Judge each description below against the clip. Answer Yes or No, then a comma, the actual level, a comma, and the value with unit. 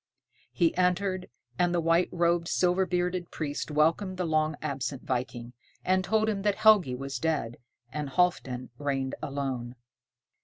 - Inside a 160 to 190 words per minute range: No, average, 145 wpm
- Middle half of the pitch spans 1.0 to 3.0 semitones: No, average, 5.0 semitones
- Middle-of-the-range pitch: Yes, medium, 165 Hz